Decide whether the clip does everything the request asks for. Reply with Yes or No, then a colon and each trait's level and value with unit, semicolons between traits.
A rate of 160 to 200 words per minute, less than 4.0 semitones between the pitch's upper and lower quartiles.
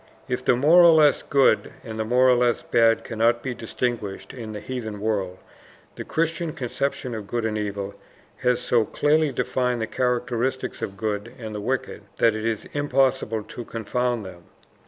Yes: average, 180 wpm; average, 2.9 semitones